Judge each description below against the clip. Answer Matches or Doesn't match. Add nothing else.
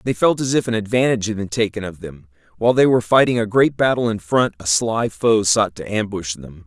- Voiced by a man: Matches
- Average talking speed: Doesn't match